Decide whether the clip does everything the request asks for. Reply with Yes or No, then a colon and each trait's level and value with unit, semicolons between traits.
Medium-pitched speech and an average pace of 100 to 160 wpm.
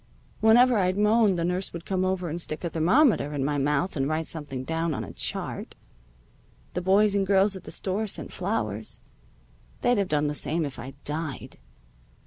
No: medium, 175 Hz; average, 190 wpm